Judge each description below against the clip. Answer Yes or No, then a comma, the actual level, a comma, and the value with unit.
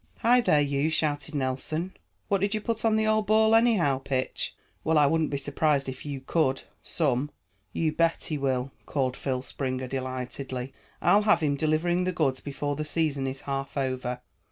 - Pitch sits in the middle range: Yes, medium, 145 Hz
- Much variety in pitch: No, average, 4.0 semitones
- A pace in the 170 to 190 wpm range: Yes, average, 180 wpm